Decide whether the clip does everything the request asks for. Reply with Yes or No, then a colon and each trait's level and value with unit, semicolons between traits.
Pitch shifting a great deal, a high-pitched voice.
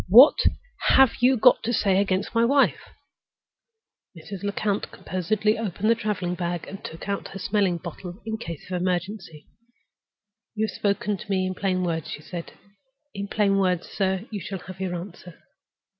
No: average, 2.9 semitones; high, 195 Hz